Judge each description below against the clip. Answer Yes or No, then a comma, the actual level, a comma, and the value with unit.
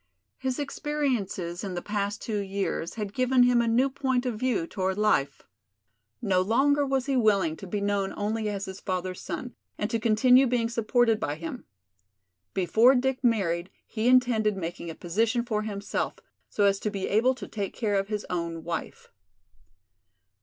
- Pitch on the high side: Yes, high, 215 Hz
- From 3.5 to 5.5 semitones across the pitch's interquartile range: Yes, average, 4.3 semitones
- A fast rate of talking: No, average, 175 wpm